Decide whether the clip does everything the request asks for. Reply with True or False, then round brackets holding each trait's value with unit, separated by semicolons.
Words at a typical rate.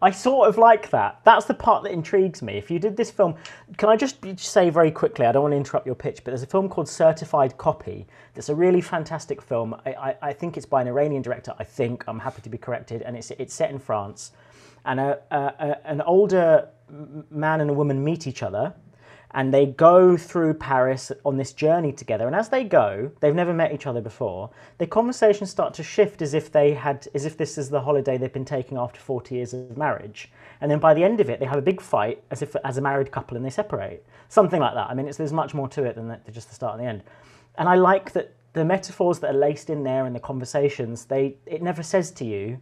False (250 wpm)